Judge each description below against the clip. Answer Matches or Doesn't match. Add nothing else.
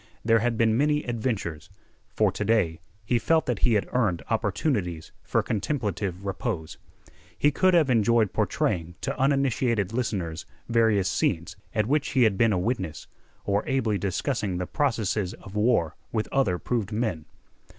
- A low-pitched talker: Matches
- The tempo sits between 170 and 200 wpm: Doesn't match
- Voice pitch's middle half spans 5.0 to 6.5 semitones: Doesn't match